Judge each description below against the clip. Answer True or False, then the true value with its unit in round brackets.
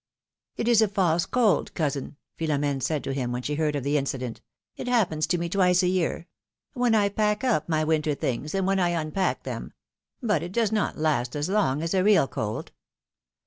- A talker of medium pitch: True (165 Hz)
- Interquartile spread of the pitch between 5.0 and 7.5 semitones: True (5.3 semitones)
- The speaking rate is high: True (215 wpm)